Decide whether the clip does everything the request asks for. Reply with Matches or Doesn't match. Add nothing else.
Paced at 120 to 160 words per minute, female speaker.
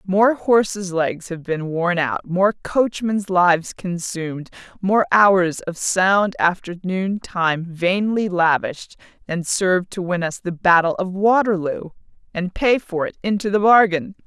Matches